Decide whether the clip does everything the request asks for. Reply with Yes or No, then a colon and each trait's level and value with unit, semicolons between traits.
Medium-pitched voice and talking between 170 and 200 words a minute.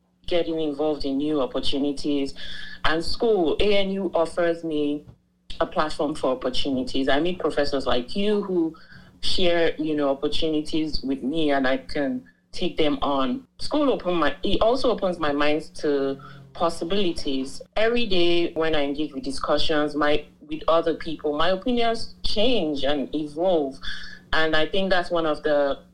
No: medium, 155 Hz; average, 150 wpm